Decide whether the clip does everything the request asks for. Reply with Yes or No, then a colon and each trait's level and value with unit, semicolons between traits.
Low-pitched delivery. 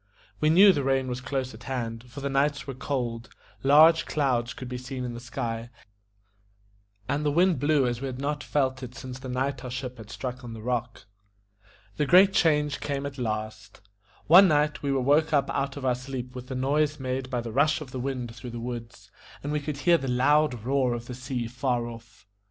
Yes: low, 130 Hz